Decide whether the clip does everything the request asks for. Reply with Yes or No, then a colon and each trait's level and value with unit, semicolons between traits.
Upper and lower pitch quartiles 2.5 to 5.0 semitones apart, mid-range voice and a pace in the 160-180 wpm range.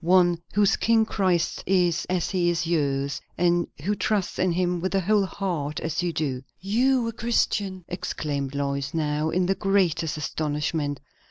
Yes: average, 4.2 semitones; medium, 175 Hz; average, 165 wpm